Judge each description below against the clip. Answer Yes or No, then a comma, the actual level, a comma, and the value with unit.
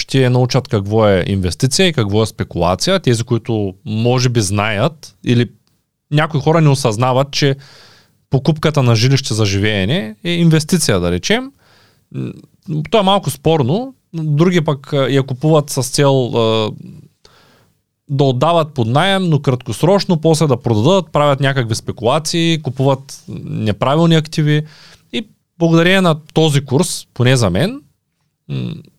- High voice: No, medium, 140 Hz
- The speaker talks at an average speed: Yes, average, 130 wpm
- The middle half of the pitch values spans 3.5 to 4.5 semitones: No, average, 5.2 semitones